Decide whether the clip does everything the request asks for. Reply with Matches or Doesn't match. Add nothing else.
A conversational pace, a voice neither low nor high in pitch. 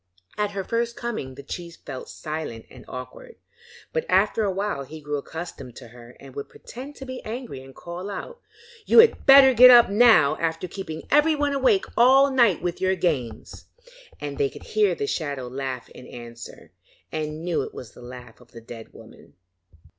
Matches